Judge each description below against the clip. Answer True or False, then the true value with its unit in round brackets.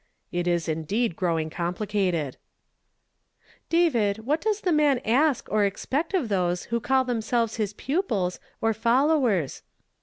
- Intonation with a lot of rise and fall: True (7.0 semitones)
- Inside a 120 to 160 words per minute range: True (150 wpm)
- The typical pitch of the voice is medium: False (220 Hz)